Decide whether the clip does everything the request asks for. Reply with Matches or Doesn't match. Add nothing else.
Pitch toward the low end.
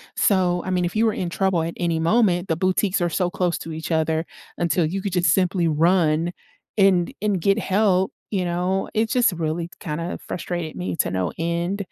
Doesn't match